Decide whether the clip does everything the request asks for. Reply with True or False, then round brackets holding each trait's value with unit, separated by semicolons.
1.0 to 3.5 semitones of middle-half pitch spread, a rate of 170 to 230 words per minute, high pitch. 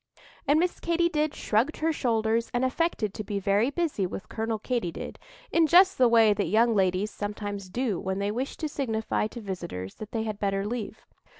False (4.8 semitones; 200 wpm; 220 Hz)